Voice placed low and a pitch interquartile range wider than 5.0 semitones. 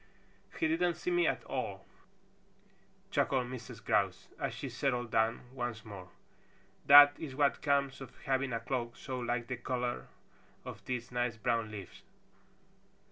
No: low, 125 Hz; average, 2.8 semitones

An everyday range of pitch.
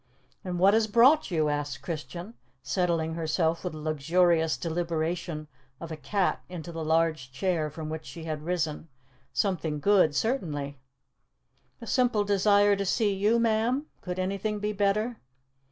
Yes: average, 4.4 semitones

